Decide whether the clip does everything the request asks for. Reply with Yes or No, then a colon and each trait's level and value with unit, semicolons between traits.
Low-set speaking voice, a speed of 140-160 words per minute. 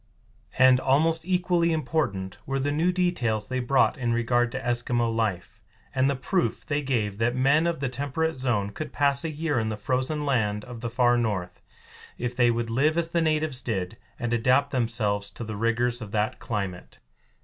No: low, 125 Hz; average, 190 wpm